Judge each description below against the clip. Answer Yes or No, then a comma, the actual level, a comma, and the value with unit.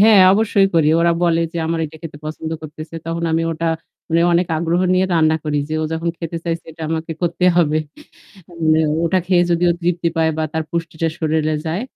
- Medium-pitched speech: Yes, medium, 165 Hz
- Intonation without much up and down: Yes, narrow, 1.4 semitones